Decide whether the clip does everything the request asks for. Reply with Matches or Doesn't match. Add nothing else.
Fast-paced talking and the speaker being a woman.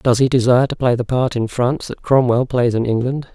Doesn't match